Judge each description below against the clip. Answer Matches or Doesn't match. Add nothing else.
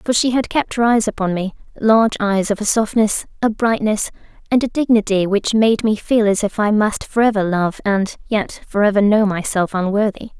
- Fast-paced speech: Matches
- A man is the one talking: Doesn't match